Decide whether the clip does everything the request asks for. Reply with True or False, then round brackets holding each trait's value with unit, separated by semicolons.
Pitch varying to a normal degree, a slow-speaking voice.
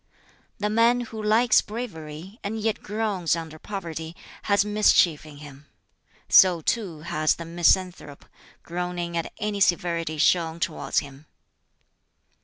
True (4.6 semitones; 125 wpm)